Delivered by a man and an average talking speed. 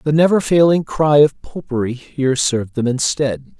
Yes: male; average, 185 wpm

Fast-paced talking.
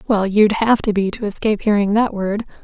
Yes: fast, 230 wpm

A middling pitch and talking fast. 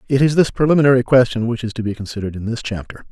No: low, 120 Hz; fast, 250 wpm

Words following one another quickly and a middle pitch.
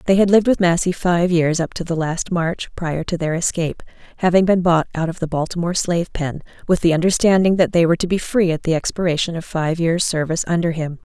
Yes: fast, 230 wpm; medium, 170 Hz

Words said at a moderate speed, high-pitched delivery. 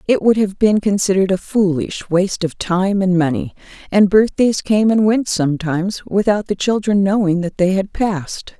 Yes: average, 180 wpm; high, 195 Hz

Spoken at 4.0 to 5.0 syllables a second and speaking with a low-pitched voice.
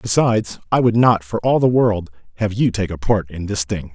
No: 5.2 syllables/s; low, 100 Hz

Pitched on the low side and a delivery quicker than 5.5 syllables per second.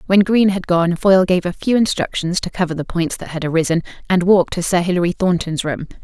No: medium, 180 Hz; 6.0 syllables/s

